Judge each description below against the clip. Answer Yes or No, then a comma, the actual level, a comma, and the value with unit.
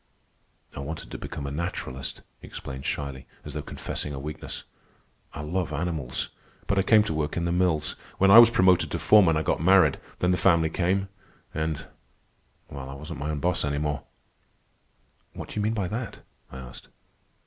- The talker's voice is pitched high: No, very low, 80 Hz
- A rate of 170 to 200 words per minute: Yes, average, 190 wpm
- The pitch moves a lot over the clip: No, average, 4.2 semitones